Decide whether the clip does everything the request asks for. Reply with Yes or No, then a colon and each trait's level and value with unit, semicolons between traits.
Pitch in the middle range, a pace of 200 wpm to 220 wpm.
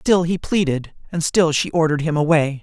Yes: medium, 160 Hz; fast, 205 wpm